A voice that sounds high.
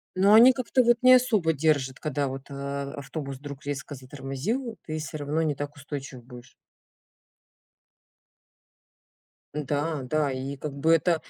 No: medium, 145 Hz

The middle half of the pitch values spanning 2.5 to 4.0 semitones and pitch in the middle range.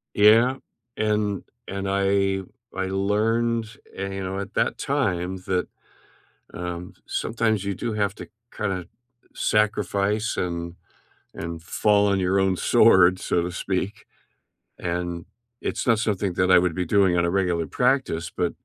No: average, 2.8 semitones; very low, 95 Hz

